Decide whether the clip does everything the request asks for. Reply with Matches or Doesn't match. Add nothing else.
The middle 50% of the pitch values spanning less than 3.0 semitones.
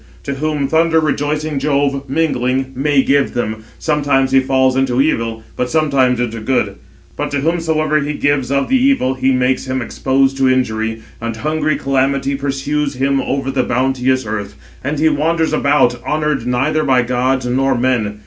Matches